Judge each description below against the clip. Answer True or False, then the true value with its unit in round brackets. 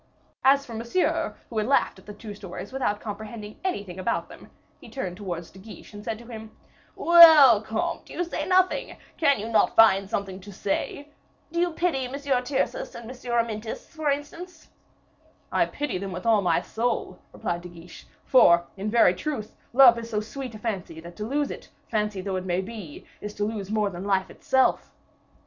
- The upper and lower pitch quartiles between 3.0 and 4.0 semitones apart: False (5.4 semitones)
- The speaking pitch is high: True (220 Hz)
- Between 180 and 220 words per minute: True (195 wpm)